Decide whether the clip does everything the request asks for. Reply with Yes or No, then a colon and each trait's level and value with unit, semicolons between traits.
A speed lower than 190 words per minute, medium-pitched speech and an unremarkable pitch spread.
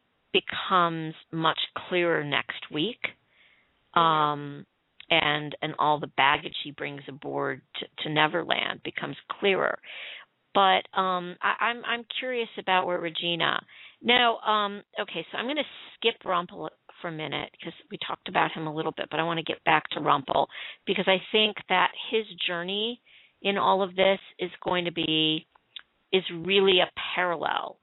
Yes: average, 160 wpm; medium, 180 Hz; average, 3.8 semitones